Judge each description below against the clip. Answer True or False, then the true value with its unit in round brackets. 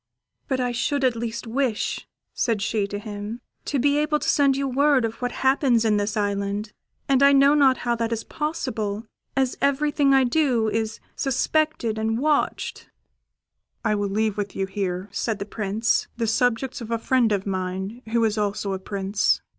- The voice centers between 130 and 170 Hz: False (230 Hz)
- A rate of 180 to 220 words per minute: True (185 wpm)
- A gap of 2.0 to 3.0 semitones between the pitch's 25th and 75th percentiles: False (4.5 semitones)